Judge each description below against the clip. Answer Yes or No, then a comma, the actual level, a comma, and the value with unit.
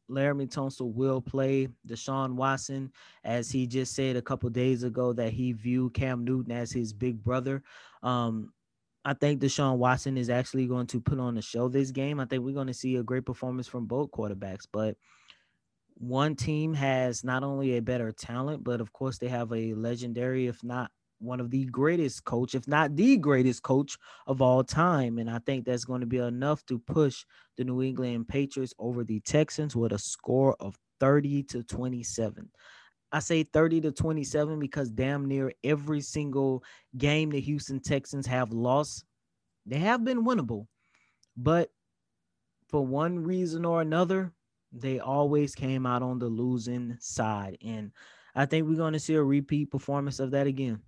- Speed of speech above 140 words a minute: Yes, average, 180 wpm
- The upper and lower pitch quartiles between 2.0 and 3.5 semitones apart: Yes, narrow, 2.5 semitones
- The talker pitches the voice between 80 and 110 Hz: No, low, 130 Hz